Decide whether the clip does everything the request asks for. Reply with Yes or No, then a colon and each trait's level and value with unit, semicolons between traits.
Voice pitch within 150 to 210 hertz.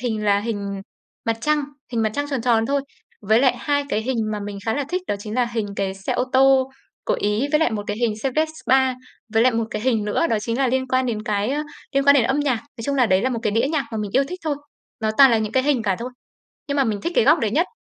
No: high, 240 Hz